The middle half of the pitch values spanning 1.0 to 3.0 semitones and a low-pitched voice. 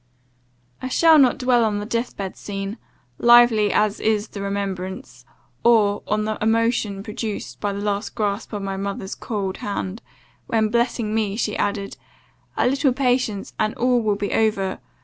No: average, 2.7 semitones; high, 210 Hz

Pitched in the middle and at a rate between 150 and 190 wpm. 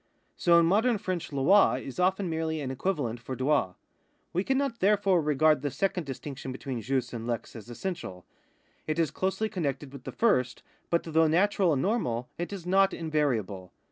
Yes: medium, 155 Hz; average, 175 wpm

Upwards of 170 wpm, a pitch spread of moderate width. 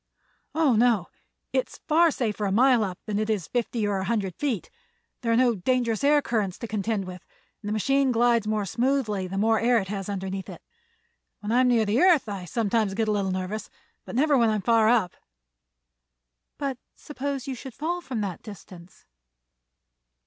Yes: average, 190 wpm; average, 3.9 semitones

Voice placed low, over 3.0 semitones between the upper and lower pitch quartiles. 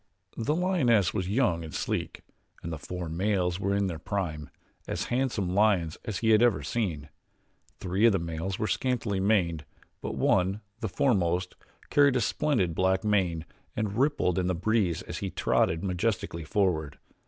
Yes: very low, 95 Hz; average, 4.3 semitones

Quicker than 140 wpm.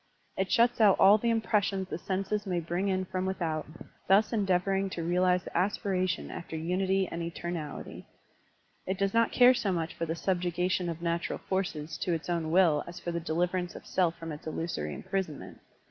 Yes: average, 190 wpm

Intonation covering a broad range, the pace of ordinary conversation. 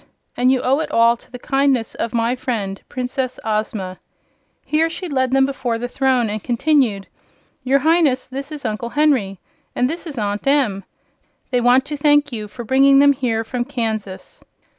No: average, 3.4 semitones; average, 180 wpm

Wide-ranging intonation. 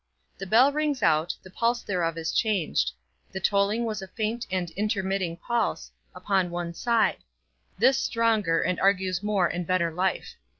No: average, 4.0 semitones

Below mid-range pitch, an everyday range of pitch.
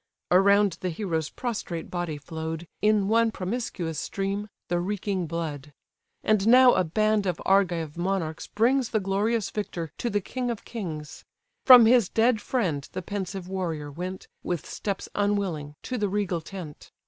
No: high, 195 Hz; average, 4.2 semitones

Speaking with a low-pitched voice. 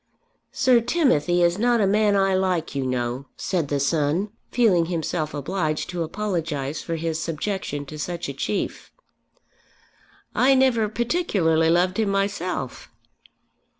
No: medium, 175 Hz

